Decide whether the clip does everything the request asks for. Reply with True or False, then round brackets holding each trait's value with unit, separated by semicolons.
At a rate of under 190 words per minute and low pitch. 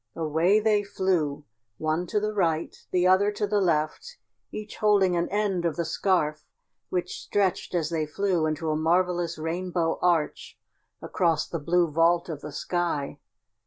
False (160 wpm; 175 Hz)